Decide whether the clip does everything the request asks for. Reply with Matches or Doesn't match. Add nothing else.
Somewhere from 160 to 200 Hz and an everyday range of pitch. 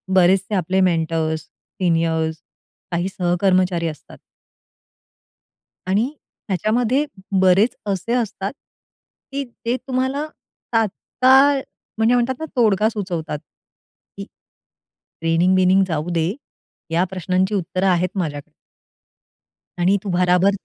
Matches